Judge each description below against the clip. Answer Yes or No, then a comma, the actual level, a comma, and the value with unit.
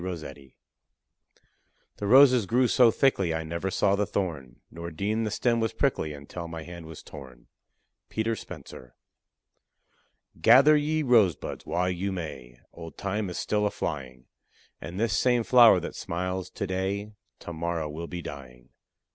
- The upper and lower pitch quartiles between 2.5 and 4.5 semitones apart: No, average, 5.3 semitones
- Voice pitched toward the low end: Yes, very low, 90 Hz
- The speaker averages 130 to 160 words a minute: Yes, average, 155 wpm